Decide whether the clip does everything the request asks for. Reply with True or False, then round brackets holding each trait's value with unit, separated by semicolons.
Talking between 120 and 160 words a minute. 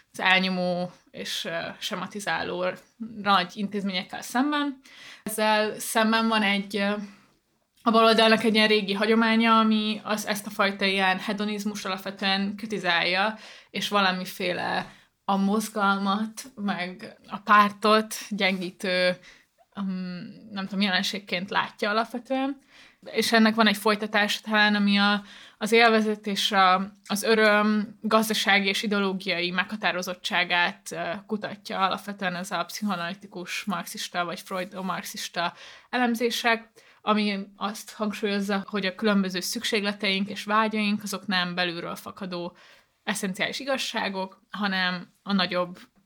False (110 wpm)